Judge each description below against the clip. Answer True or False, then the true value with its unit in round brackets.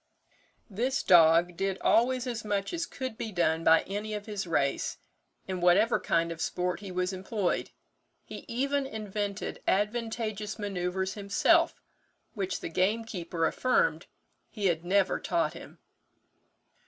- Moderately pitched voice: False (200 Hz)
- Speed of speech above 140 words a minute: False (135 wpm)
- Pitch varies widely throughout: False (3.7 semitones)